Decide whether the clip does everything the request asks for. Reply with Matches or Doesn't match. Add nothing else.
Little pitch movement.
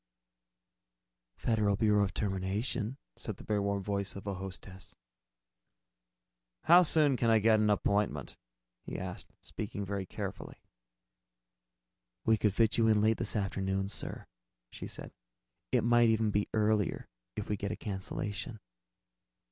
Matches